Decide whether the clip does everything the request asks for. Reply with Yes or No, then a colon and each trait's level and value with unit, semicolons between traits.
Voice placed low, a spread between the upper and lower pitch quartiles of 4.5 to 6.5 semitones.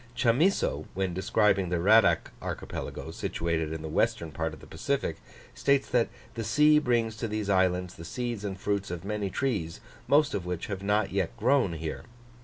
Yes: low, 100 Hz; wide, 5.4 semitones